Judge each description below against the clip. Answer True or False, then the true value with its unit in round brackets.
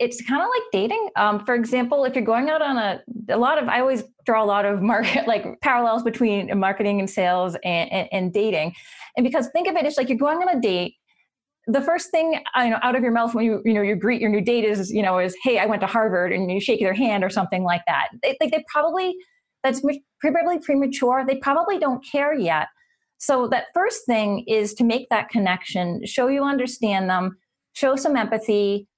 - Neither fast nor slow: False (230 wpm)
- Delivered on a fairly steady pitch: False (5.6 semitones)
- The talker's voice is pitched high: True (235 Hz)